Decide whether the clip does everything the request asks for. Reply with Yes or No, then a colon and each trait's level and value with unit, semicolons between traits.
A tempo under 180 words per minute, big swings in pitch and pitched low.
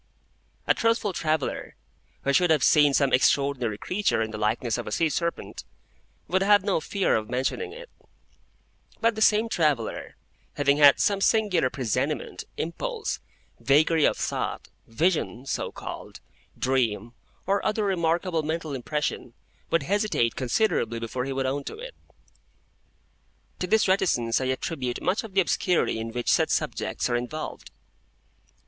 No: average, 145 wpm; wide, 7.0 semitones; medium, 155 Hz